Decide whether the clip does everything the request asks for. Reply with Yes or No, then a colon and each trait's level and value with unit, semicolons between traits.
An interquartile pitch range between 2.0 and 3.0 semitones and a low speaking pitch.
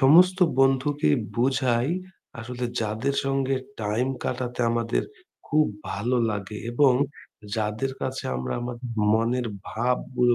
Yes: average, 2.7 semitones; low, 125 Hz